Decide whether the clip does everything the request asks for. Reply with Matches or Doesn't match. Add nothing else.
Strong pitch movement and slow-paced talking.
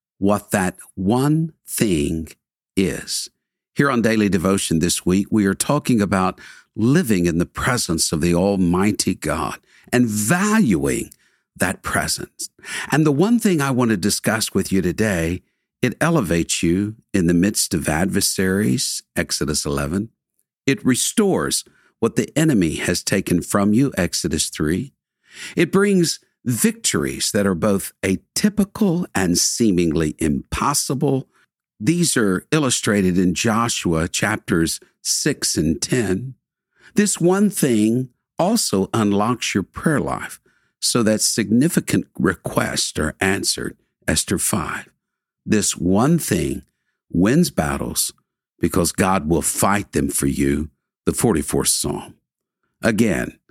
Matches